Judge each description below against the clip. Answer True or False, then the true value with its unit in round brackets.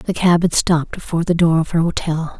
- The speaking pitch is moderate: True (165 Hz)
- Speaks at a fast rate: True (250 wpm)